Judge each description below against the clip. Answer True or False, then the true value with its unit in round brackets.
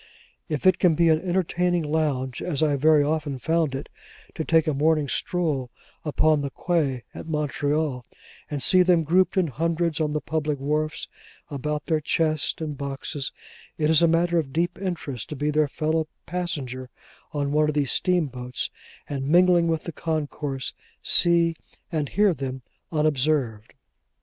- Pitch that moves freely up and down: False (2.8 semitones)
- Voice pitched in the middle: True (155 Hz)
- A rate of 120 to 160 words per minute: True (155 wpm)